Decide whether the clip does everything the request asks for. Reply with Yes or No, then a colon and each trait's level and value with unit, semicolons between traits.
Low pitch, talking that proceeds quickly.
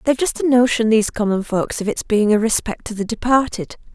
No: high, 225 Hz; fast, 230 wpm